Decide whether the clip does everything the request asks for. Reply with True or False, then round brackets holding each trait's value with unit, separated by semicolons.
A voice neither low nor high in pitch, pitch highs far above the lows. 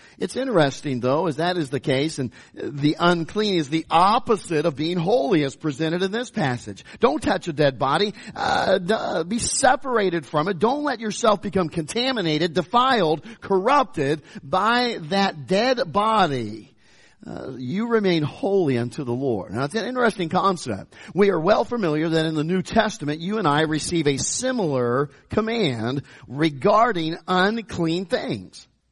True (175 Hz; 6.1 semitones)